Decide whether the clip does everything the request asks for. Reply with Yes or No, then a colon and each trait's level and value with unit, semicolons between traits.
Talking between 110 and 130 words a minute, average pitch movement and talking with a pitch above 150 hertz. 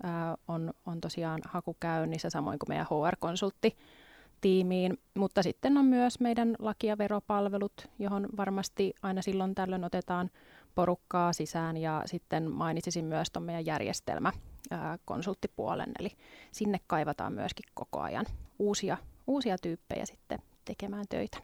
Yes: average, 125 wpm; average, 3.3 semitones; medium, 185 Hz